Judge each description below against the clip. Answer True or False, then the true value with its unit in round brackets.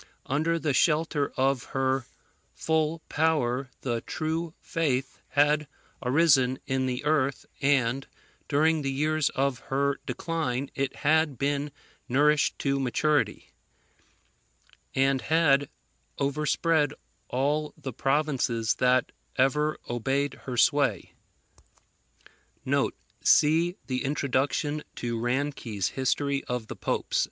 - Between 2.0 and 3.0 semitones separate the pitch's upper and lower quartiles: True (2.6 semitones)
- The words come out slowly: True (105 wpm)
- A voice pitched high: False (140 Hz)